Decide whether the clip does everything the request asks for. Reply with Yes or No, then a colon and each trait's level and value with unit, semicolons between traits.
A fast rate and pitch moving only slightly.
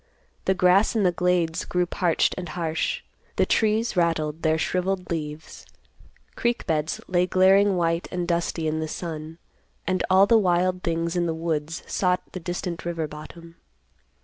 No: average, 160 wpm; narrow, 2.1 semitones